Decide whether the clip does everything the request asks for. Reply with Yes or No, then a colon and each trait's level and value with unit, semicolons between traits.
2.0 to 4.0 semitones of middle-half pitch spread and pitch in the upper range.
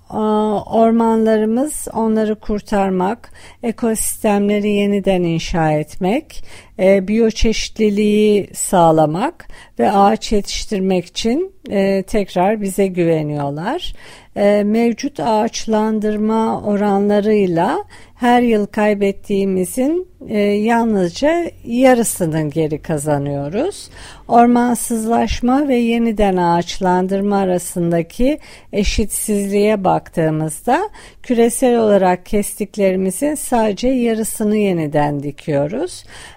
Yes: average, 3.6 semitones; high, 210 Hz